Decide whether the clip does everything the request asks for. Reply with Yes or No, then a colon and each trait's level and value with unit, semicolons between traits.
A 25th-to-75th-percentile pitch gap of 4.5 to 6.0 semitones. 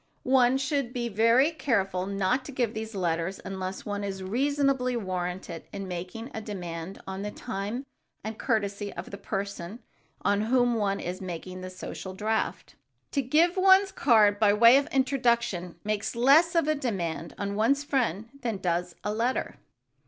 Yes: average, 5.0 semitones